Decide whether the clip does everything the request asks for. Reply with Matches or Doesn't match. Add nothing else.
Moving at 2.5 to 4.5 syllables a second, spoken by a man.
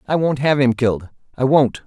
Doesn't match